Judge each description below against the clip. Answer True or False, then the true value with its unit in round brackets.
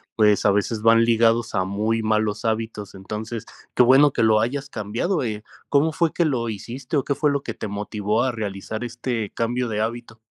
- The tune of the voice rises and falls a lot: False (2.5 semitones)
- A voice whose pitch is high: False (115 Hz)